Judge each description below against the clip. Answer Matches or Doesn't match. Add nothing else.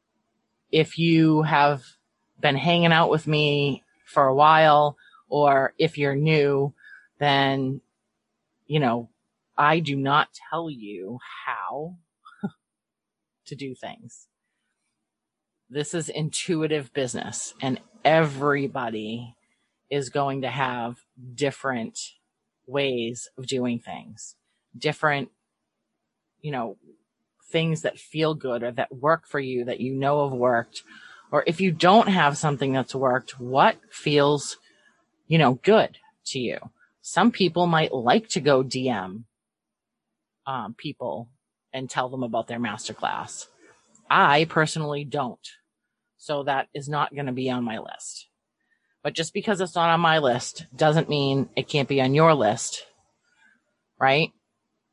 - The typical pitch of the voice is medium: Matches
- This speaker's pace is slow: Matches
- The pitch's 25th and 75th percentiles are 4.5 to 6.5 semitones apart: Doesn't match